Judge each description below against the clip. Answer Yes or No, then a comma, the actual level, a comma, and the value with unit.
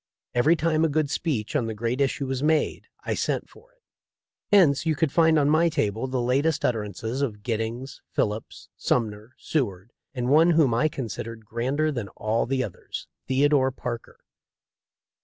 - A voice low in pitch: Yes, low, 130 Hz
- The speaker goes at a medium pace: Yes, average, 175 wpm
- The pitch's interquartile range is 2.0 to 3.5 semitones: No, average, 5.1 semitones